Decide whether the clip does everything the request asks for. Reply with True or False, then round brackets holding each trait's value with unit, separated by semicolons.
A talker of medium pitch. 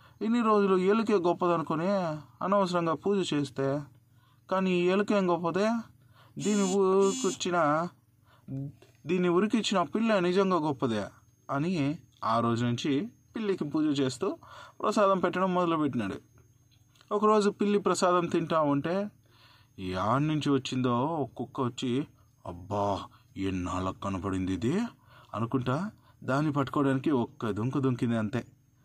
True (145 Hz)